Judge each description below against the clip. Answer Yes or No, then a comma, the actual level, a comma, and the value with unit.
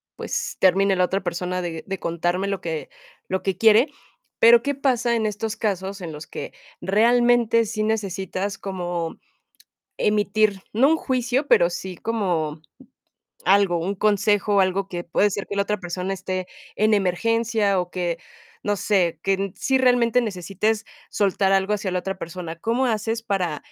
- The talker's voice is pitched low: No, high, 195 Hz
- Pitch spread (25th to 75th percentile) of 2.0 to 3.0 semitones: No, average, 3.4 semitones